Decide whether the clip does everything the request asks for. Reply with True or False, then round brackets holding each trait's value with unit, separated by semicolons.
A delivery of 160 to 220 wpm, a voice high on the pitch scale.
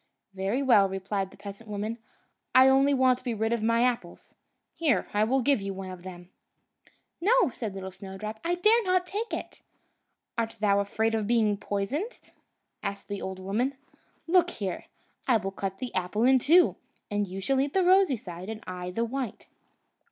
True (180 wpm; 220 Hz)